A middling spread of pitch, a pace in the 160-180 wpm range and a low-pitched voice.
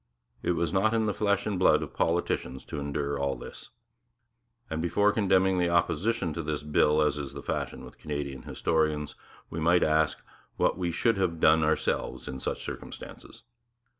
Yes: average, 3.9 semitones; average, 175 wpm; very low, 80 Hz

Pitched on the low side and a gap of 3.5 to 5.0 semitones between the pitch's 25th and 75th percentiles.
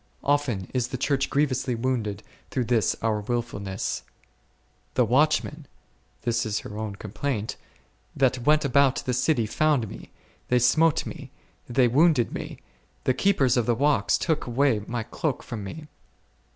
Yes: low, 125 Hz; average, 3.9 semitones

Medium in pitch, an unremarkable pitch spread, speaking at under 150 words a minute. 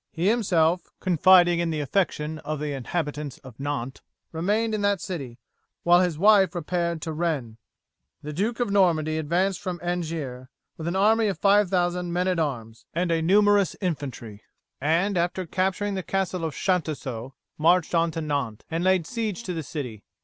No: medium, 170 Hz; average, 3.8 semitones; average, 165 wpm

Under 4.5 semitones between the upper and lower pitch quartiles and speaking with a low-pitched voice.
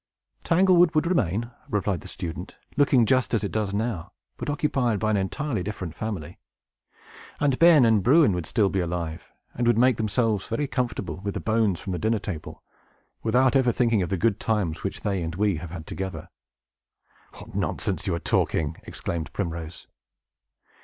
No: wide, 5.5 semitones; low, 105 Hz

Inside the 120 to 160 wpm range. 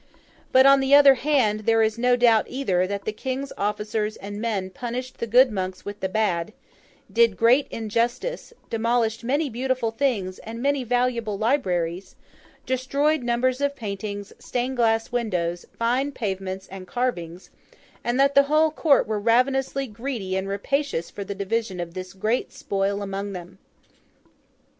Yes: average, 155 wpm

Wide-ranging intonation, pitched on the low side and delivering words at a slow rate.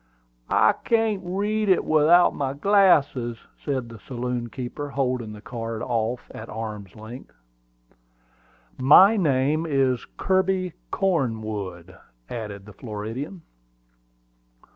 Yes: wide, 7.3 semitones; low, 130 Hz; slow, 105 wpm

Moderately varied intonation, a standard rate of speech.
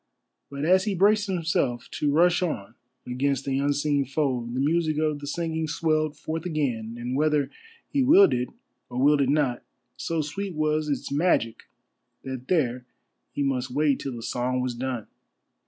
Yes: average, 3.8 semitones; average, 170 wpm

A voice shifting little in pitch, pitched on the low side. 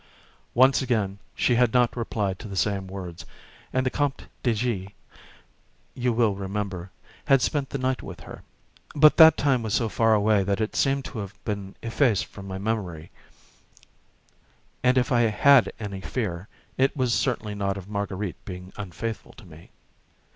No: average, 4.4 semitones; low, 110 Hz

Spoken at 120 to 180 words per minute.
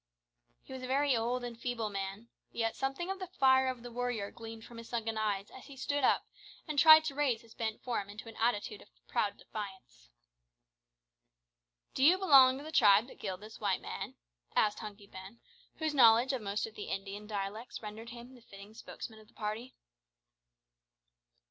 No: average, 190 wpm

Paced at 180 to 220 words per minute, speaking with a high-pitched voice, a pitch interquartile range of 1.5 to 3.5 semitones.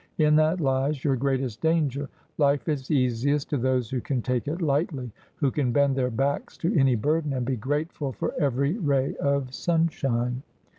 No: average, 185 wpm; medium, 140 Hz; average, 2.7 semitones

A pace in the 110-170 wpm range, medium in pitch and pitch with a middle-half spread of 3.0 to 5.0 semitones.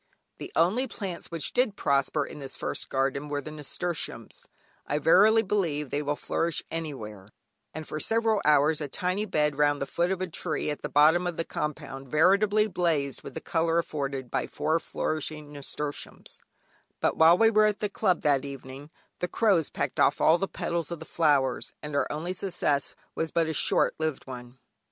No: average, 190 wpm; medium, 155 Hz; average, 3.8 semitones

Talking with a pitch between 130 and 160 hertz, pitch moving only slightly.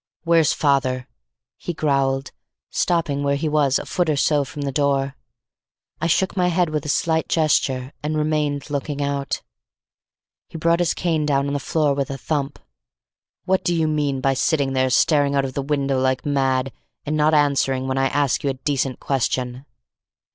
Yes: medium, 140 Hz; narrow, 2.3 semitones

